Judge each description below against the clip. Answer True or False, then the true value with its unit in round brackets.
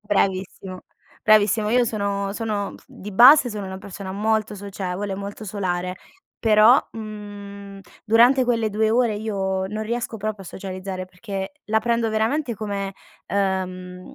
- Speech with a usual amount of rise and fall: False (2.3 semitones)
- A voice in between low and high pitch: False (205 Hz)